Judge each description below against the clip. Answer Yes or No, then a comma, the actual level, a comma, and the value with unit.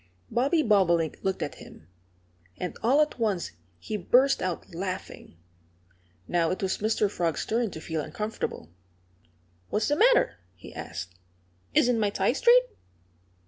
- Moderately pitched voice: No, high, 205 Hz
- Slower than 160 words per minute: Yes, average, 140 wpm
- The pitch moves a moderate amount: No, wide, 6.1 semitones